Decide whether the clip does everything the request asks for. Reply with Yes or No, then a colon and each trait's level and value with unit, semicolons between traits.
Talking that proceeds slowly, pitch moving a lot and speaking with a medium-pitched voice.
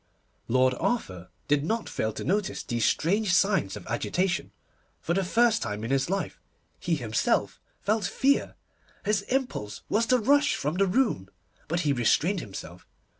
No: average, 165 wpm; wide, 9.0 semitones; medium, 180 Hz